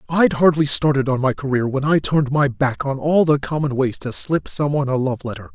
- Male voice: Yes, male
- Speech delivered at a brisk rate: Yes, fast, 240 wpm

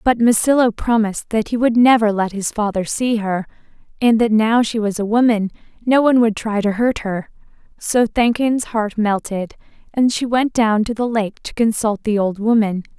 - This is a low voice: No, high, 220 Hz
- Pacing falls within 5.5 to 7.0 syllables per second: No, 5.0 syllables/s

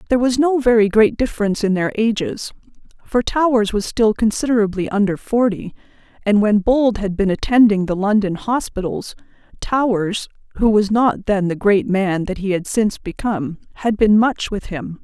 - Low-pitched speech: No, high, 210 Hz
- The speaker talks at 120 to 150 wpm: No, average, 170 wpm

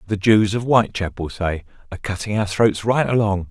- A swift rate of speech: No, average, 190 wpm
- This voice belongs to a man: Yes, male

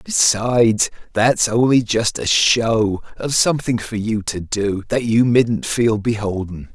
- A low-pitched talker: Yes, low, 110 Hz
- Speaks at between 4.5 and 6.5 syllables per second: No, 3.9 syllables/s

